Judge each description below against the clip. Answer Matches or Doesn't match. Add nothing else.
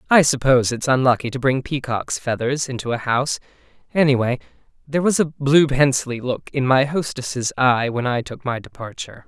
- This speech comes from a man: Matches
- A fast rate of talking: Doesn't match